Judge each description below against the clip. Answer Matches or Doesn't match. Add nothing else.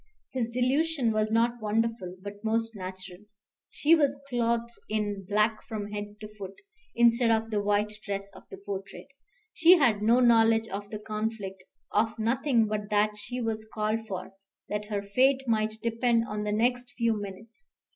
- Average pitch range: Doesn't match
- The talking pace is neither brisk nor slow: Matches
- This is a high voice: Matches